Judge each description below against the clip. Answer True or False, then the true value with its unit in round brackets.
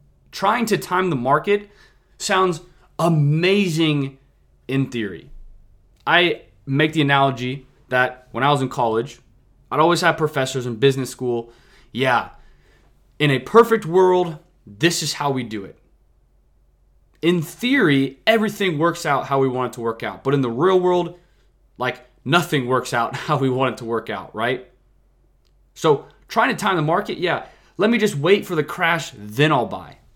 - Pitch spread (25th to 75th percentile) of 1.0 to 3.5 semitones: False (5.6 semitones)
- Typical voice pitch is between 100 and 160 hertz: True (140 Hz)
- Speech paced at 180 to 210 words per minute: False (165 wpm)